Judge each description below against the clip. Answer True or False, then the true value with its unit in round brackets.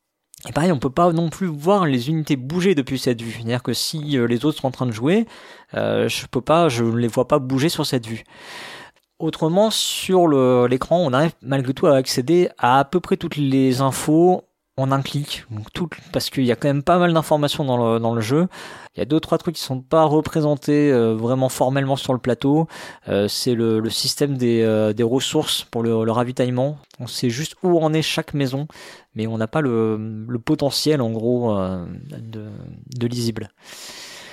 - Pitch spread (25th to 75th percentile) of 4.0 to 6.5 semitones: True (4.7 semitones)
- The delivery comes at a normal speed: True (210 wpm)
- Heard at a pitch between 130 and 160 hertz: True (135 Hz)